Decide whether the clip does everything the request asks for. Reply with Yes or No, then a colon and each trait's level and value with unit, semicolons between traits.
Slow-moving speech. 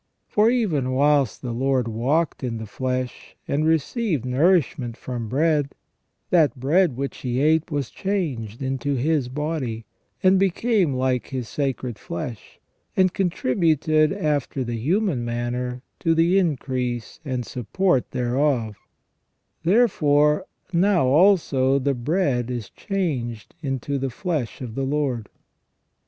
Yes: slow, 125 wpm